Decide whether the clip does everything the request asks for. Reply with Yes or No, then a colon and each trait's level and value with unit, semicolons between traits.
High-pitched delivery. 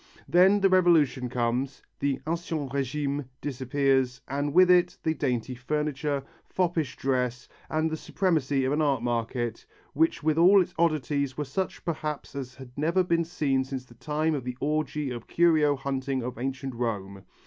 No: medium, 140 Hz